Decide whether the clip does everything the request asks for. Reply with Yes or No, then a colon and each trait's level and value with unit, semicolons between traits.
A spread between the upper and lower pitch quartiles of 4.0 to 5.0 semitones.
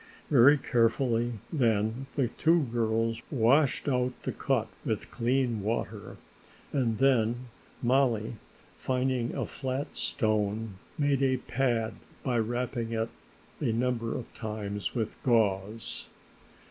No: average, 2.7 semitones